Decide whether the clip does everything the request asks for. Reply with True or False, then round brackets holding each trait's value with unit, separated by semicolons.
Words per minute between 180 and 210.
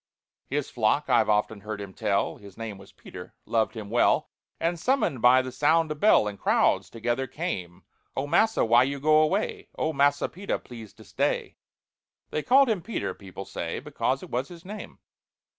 True (185 wpm)